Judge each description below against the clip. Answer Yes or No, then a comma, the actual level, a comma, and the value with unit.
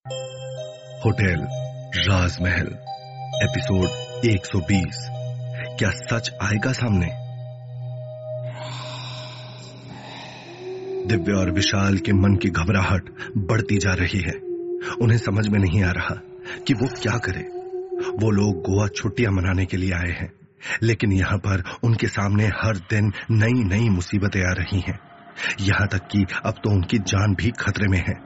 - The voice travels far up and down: No, average, 4.2 semitones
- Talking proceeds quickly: No, average, 135 wpm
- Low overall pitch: Yes, low, 110 Hz